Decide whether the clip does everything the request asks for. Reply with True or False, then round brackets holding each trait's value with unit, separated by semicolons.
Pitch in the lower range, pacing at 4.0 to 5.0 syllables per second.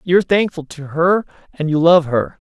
False (165 Hz; 4.9 syllables/s)